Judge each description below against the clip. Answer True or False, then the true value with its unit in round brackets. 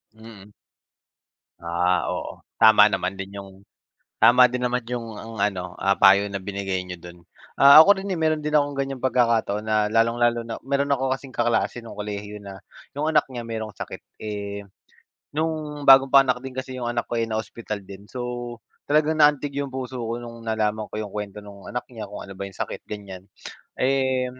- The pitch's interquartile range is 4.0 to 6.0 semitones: True (4.4 semitones)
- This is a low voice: True (115 Hz)